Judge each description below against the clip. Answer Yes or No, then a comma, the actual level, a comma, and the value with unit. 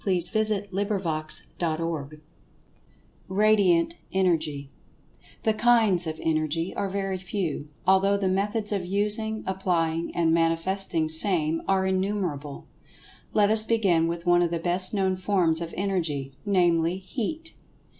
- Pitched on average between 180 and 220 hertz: Yes, medium, 185 Hz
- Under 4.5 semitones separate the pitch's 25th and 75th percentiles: Yes, average, 3.4 semitones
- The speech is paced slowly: Yes, slow, 125 wpm